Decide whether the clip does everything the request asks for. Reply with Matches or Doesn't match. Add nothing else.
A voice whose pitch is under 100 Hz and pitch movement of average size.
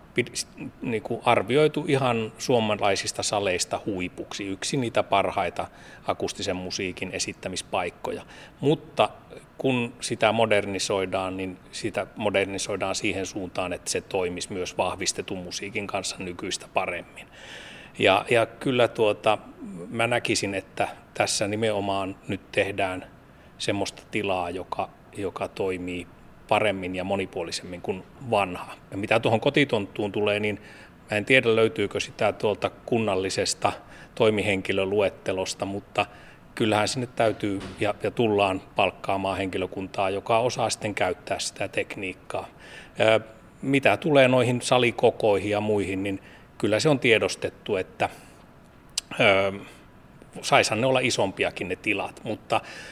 Doesn't match